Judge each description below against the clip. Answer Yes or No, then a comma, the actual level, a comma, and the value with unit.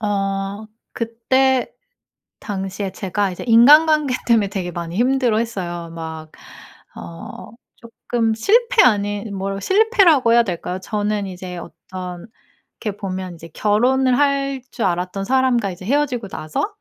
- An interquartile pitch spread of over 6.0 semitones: No, wide, 5.4 semitones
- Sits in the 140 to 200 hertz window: No, high, 210 Hz